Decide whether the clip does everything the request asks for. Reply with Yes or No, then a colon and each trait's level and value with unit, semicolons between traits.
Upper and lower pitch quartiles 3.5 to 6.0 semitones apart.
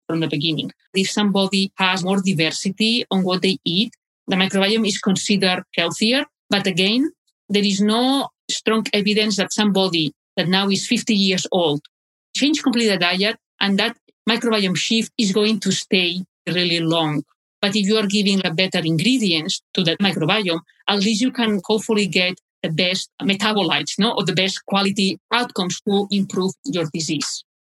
No: average, 3.0 semitones